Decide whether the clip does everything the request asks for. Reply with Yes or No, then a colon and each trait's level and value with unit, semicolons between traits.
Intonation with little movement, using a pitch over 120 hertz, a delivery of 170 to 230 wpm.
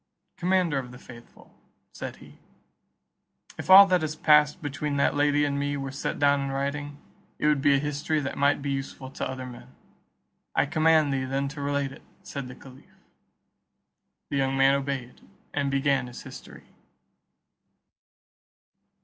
No: narrow, 1.4 semitones; medium, 140 Hz; average, 160 wpm